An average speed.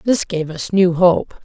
No: fast, 210 wpm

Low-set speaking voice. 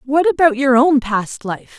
No: very high, 265 Hz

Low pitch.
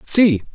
No: medium, 170 Hz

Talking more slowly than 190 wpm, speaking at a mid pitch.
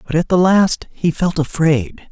No: average, 200 wpm; medium, 160 Hz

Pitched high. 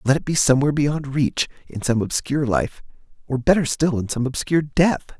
No: medium, 140 Hz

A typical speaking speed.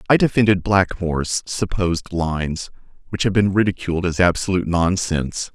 No: slow, 130 wpm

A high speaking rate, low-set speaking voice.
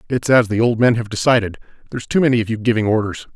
Yes: fast, 235 wpm; low, 115 Hz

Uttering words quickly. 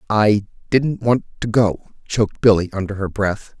No: slow, 135 wpm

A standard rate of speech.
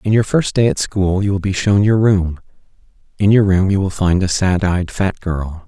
No: fast, 245 wpm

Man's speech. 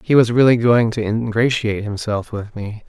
Yes: male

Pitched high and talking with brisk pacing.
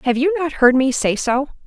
Yes: very high, 265 Hz; fast, 250 wpm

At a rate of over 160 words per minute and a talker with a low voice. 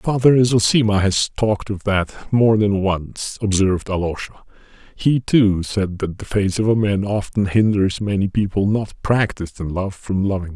Yes: average, 175 wpm; low, 100 Hz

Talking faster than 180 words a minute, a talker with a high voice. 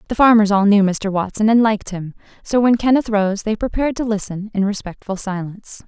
Yes: fast, 205 wpm; high, 210 Hz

